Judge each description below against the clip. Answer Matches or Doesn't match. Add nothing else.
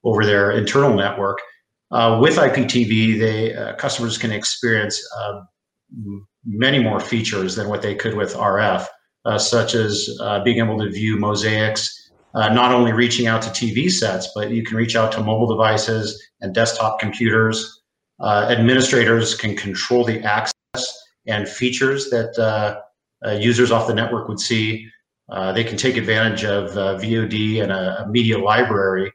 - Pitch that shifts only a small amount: Matches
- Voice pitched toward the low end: Matches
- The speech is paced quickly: Doesn't match